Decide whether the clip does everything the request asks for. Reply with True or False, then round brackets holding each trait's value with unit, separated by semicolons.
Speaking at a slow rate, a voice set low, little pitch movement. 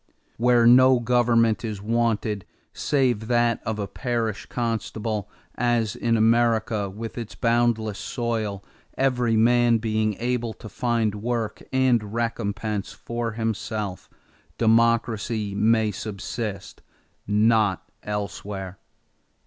True (105 wpm; 115 Hz; 2.0 semitones)